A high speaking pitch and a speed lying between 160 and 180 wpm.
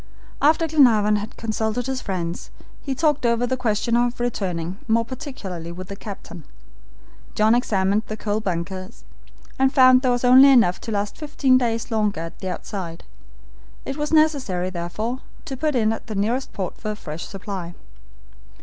Yes: high, 220 Hz; average, 170 wpm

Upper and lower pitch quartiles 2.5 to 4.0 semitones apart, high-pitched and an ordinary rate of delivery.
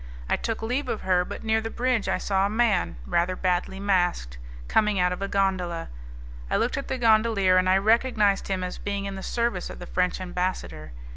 No: average, 3.4 semitones; high, 195 Hz; fast, 210 wpm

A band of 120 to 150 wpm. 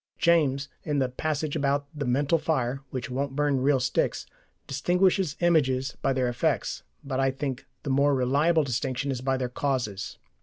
No: average, 165 wpm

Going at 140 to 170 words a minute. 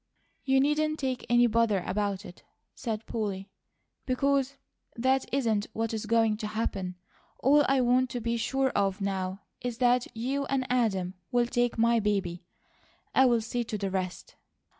Yes: average, 160 wpm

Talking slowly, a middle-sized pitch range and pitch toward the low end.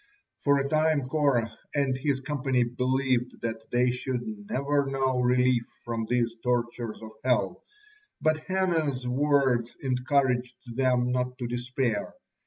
No: slow, 130 wpm; narrow, 2.2 semitones; low, 125 Hz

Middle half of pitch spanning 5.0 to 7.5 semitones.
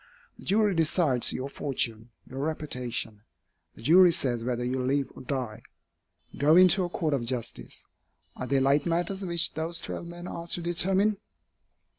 Yes: wide, 5.4 semitones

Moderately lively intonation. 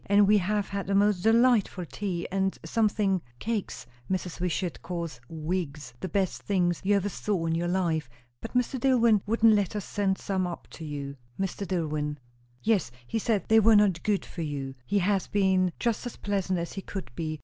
Yes: average, 3.3 semitones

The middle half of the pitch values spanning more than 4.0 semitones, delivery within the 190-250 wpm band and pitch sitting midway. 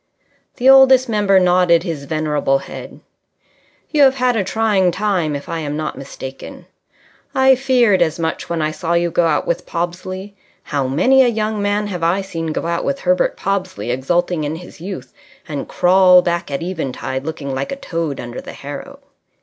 No: average, 4.6 semitones; average, 180 wpm; medium, 175 Hz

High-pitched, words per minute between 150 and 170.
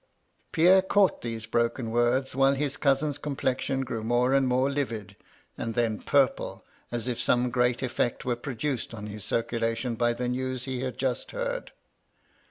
No: low, 125 Hz; average, 165 wpm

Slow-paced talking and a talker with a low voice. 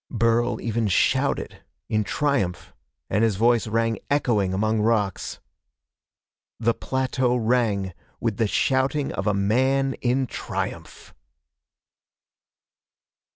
Yes: slow, 105 wpm; low, 115 Hz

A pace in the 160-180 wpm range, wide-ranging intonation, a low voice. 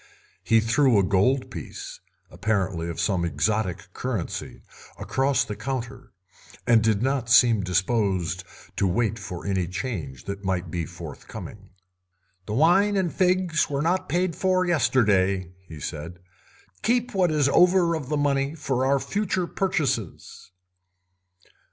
No: slow, 135 wpm; wide, 8.2 semitones; low, 115 Hz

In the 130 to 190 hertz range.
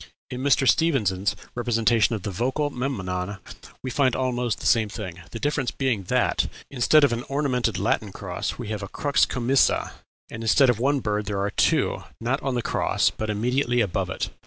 No: low, 120 Hz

